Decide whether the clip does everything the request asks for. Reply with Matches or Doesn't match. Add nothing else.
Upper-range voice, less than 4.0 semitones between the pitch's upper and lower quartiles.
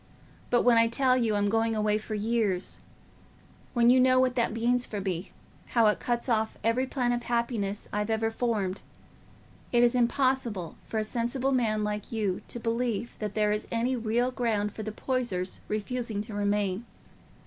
Matches